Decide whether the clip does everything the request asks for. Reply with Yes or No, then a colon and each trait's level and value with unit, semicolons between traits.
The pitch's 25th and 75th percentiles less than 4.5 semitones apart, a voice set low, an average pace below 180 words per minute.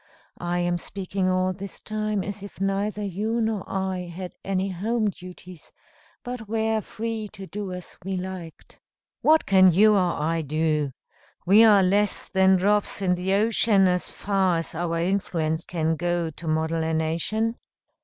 No: average, 3.1 semitones; high, 190 Hz; average, 165 wpm